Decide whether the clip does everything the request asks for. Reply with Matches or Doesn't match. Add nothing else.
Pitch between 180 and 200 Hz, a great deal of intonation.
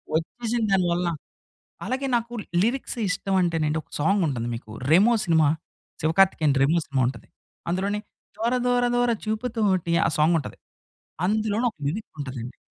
Matches